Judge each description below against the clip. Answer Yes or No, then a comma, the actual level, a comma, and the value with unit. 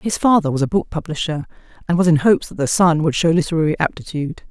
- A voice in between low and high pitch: Yes, medium, 165 Hz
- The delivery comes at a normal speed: No, fast, 225 wpm